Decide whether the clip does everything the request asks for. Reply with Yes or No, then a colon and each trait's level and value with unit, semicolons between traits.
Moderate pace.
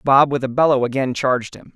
No: fast, 240 wpm